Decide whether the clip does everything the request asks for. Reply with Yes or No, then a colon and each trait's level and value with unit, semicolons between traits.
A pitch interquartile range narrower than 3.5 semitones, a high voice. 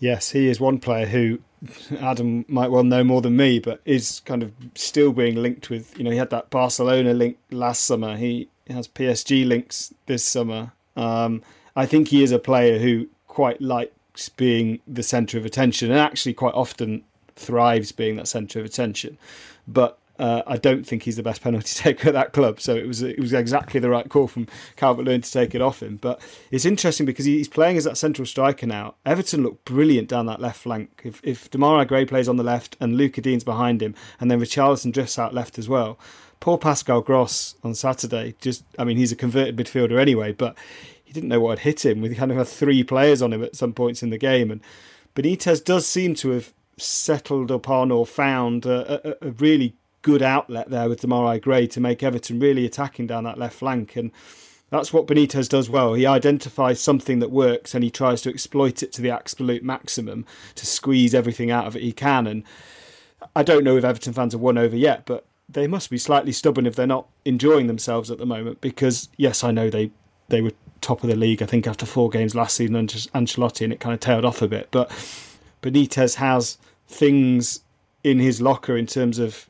No: narrow, 2.4 semitones; low, 125 Hz